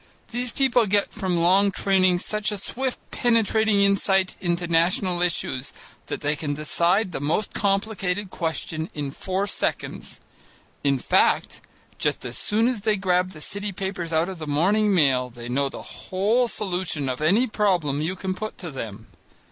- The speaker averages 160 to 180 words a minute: Yes, average, 165 wpm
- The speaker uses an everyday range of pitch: Yes, average, 4.4 semitones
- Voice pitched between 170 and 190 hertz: Yes, medium, 185 Hz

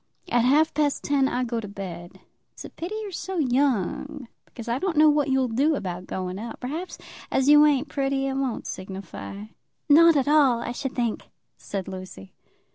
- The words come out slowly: No, average, 190 wpm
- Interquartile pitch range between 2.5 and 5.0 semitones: No, wide, 5.4 semitones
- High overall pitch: Yes, very high, 265 Hz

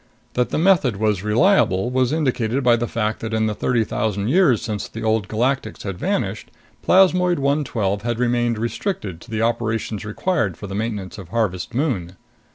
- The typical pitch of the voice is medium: No, low, 115 Hz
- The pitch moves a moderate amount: Yes, average, 3.3 semitones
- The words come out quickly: No, average, 175 wpm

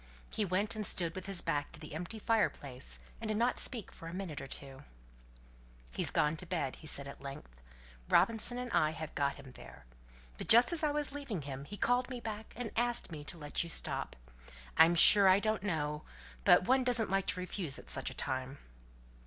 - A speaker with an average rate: No, fast, 210 wpm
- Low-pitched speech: No, medium, 185 Hz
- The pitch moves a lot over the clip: Yes, wide, 7.2 semitones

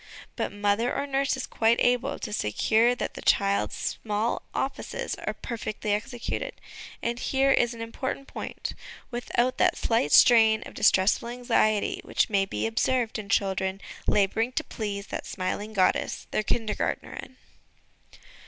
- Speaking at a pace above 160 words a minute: No, average, 145 wpm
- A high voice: Yes, high, 225 Hz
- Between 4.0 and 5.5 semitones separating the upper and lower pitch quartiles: No, average, 3.3 semitones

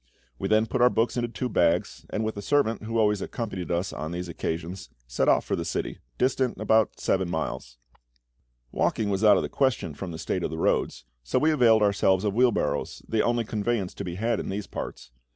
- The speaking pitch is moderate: No, low, 105 Hz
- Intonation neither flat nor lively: Yes, average, 4.6 semitones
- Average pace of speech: No, fast, 220 wpm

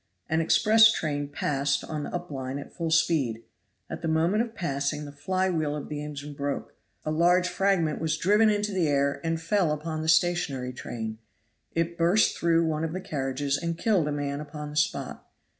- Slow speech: No, average, 195 wpm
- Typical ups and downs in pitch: Yes, average, 3.3 semitones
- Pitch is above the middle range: No, medium, 155 Hz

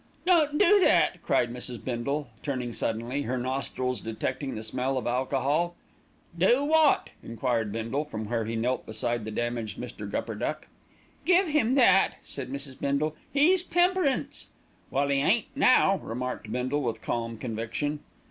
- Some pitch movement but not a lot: No, wide, 6.8 semitones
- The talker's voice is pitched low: Yes, low, 130 Hz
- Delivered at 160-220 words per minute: No, average, 145 wpm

